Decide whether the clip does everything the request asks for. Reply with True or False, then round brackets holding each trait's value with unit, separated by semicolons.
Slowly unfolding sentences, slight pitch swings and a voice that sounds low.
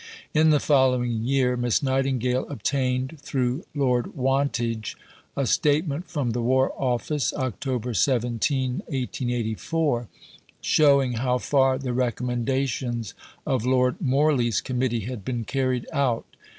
True (115 wpm; 2.0 semitones; 130 Hz)